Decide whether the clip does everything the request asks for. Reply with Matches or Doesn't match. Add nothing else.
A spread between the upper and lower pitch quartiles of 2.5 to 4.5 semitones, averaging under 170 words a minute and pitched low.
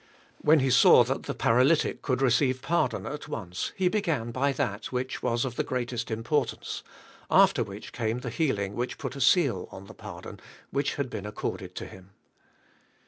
Doesn't match